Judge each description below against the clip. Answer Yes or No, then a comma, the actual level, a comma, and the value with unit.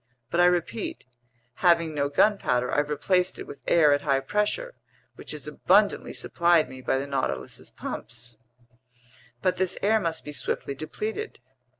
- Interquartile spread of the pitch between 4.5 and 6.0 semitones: Yes, average, 4.9 semitones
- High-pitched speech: No, medium, 160 Hz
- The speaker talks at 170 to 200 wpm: No, average, 155 wpm